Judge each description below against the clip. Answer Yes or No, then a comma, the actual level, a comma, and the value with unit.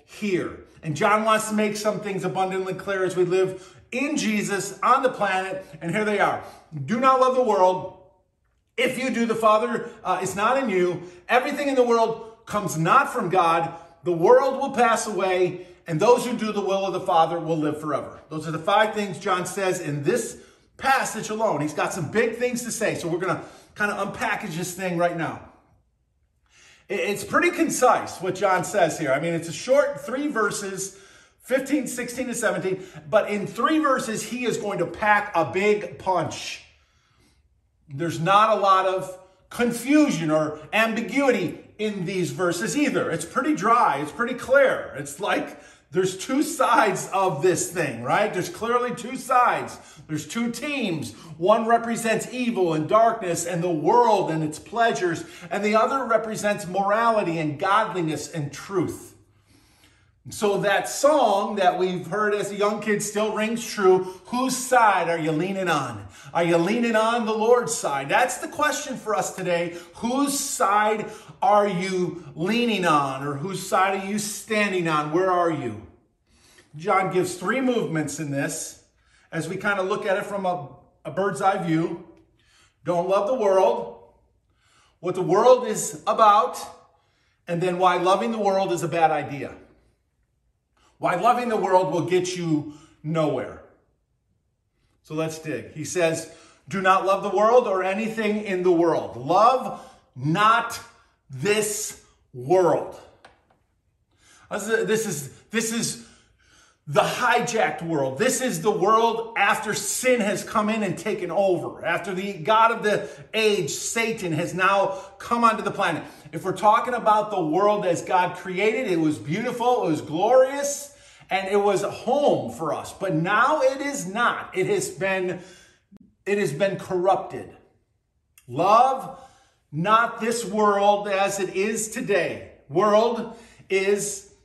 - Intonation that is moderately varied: Yes, average, 4.8 semitones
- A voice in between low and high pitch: No, high, 195 Hz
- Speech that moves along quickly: No, average, 165 wpm